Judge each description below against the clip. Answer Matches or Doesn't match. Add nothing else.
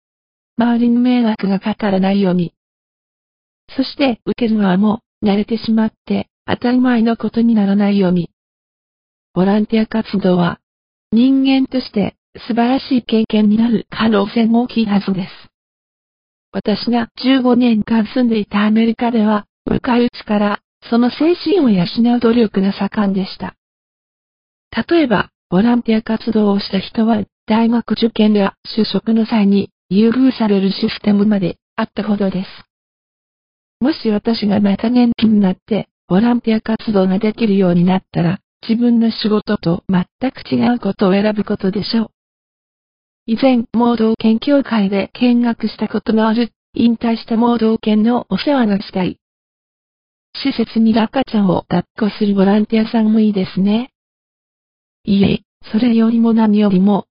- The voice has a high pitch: Matches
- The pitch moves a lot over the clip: Doesn't match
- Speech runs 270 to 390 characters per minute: Matches